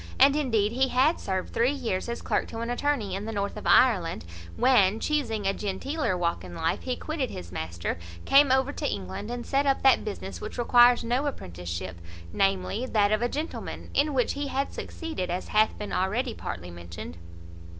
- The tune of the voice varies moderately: No, wide, 6.1 semitones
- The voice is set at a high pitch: Yes, high, 225 Hz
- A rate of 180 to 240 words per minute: Yes, average, 190 wpm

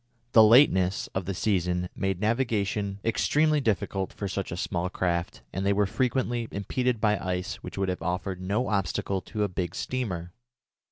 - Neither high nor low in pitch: No, low, 100 Hz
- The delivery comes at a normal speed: Yes, average, 165 wpm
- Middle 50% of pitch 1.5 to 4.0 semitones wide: Yes, average, 3.4 semitones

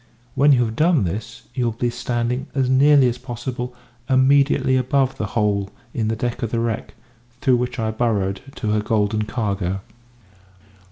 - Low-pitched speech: Yes, low, 120 Hz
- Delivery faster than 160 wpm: Yes, average, 170 wpm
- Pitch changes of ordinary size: Yes, average, 3.2 semitones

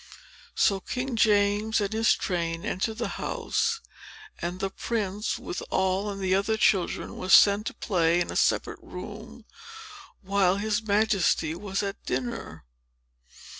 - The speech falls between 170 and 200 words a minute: No, average, 140 wpm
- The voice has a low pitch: No, high, 200 Hz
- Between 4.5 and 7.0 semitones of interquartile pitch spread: No, average, 2.8 semitones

